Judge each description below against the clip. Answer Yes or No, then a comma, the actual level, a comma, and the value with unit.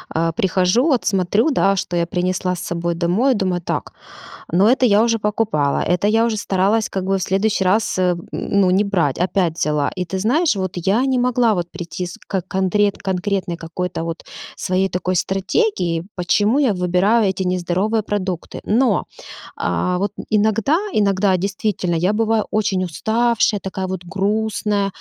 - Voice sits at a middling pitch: No, high, 195 Hz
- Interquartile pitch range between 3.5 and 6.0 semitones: No, average, 3.0 semitones